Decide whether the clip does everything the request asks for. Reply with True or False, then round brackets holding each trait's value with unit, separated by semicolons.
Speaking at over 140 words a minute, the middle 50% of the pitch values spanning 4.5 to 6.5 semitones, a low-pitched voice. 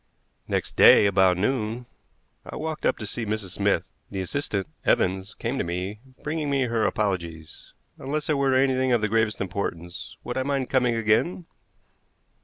True (165 wpm; 5.5 semitones; 110 Hz)